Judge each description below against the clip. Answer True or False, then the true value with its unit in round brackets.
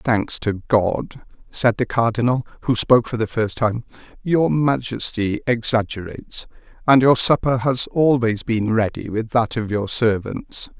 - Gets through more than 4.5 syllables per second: False (4.3 syllables/s)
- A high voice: False (115 Hz)